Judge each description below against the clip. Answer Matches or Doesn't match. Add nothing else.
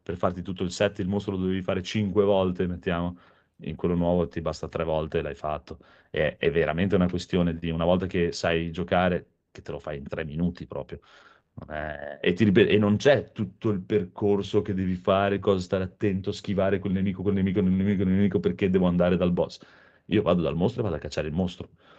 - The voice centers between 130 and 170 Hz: Doesn't match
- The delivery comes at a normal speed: Doesn't match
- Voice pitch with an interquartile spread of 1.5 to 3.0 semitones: Matches